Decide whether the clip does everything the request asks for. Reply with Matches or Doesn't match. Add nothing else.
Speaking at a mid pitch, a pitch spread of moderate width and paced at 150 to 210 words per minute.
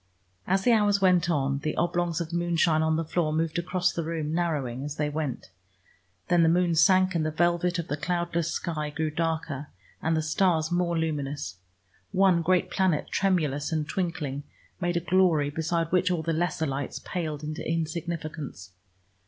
Doesn't match